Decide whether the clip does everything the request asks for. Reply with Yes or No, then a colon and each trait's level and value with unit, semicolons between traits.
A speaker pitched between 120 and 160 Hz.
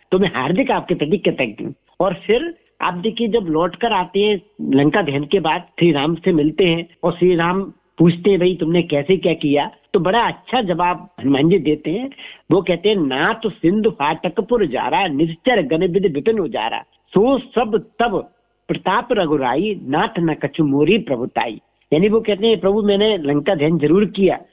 No: medium, 180 Hz